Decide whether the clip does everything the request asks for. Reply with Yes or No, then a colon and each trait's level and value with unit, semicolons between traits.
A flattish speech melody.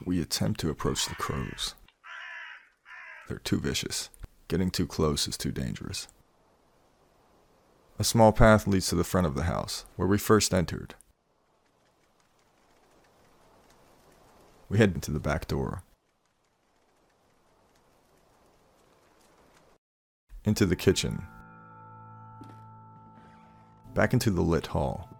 No: average, 4.0 semitones